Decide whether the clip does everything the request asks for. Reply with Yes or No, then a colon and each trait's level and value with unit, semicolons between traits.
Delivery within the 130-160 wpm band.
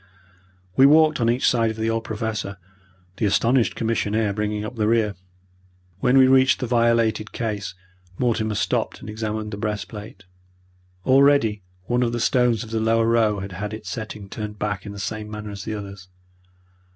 No: average, 175 wpm